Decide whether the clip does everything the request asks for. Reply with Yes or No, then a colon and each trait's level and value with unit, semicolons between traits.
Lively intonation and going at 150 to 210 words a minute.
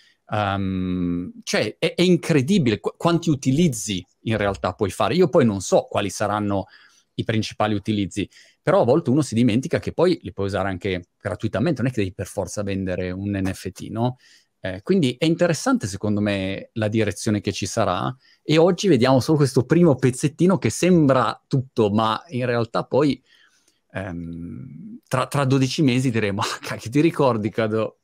Yes: wide, 6.1 semitones; fast, 170 wpm